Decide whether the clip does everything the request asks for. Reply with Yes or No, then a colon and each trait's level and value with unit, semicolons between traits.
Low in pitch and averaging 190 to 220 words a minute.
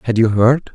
No: low, 120 Hz; fast, 240 wpm